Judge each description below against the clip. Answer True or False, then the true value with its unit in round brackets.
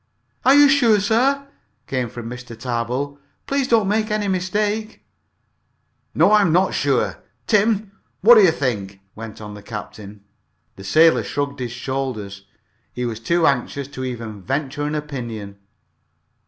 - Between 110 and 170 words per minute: True (150 wpm)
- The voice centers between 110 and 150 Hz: True (140 Hz)